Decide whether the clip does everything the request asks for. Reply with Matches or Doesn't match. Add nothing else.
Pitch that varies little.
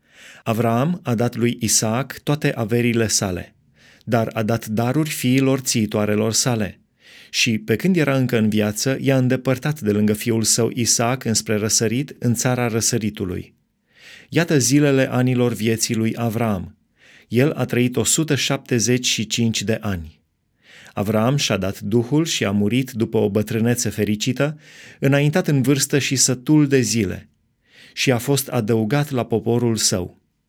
Doesn't match